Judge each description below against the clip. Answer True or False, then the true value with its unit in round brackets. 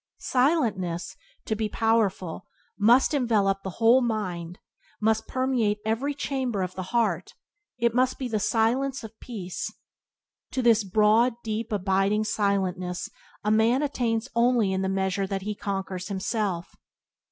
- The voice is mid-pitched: False (215 Hz)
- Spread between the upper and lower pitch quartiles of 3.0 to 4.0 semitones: True (3.6 semitones)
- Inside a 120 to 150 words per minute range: True (140 wpm)